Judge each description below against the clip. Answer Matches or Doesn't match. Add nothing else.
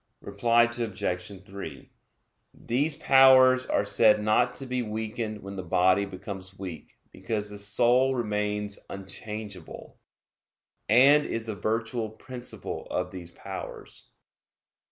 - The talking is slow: Matches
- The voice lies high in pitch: Doesn't match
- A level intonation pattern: Doesn't match